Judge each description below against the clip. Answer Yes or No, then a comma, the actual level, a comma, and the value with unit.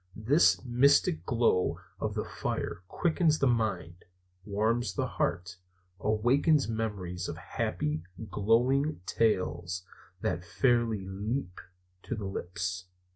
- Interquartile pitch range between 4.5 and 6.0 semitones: Yes, average, 5.1 semitones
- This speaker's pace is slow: Yes, slow, 110 wpm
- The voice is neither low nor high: No, low, 110 Hz